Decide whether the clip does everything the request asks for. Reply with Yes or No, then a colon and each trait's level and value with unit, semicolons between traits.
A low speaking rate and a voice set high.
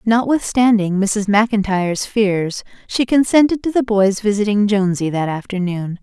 Yes: slow, 130 wpm; high, 210 Hz